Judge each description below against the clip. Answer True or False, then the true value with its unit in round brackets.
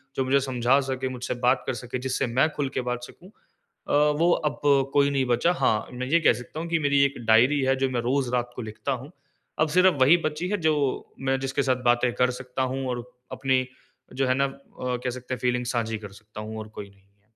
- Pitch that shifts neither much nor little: False (2.2 semitones)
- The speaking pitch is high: False (130 Hz)